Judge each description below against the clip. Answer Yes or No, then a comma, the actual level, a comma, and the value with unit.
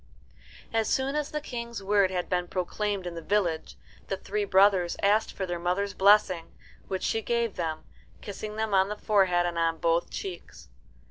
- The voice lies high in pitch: Yes, high, 195 Hz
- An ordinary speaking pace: Yes, average, 180 wpm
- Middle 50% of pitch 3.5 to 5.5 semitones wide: No, average, 3.1 semitones